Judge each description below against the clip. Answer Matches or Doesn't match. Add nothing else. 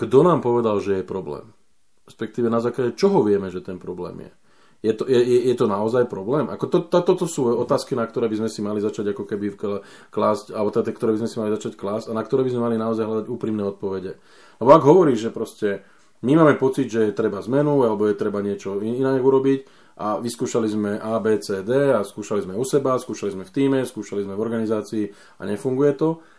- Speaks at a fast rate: Matches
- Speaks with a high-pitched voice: Doesn't match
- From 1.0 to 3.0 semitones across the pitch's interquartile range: Doesn't match